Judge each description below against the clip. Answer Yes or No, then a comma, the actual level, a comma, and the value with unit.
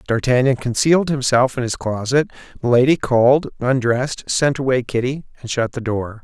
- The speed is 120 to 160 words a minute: Yes, average, 155 wpm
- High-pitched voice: No, low, 125 Hz